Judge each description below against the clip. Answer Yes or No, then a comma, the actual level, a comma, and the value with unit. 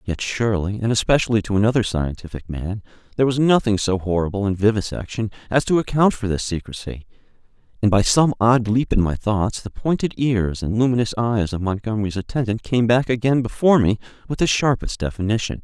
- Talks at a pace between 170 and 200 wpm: Yes, average, 180 wpm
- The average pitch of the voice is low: Yes, low, 110 Hz